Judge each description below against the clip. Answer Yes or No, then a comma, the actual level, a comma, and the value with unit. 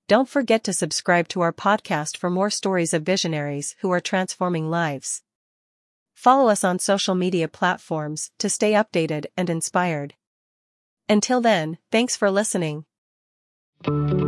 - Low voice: No, medium, 180 Hz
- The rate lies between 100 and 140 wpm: Yes, slow, 135 wpm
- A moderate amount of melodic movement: Yes, average, 4.0 semitones